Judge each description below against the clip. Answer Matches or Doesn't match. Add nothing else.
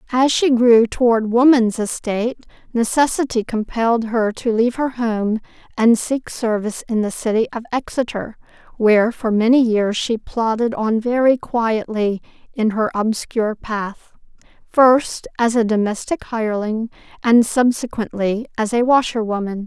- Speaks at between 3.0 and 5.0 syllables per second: Matches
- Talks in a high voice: Matches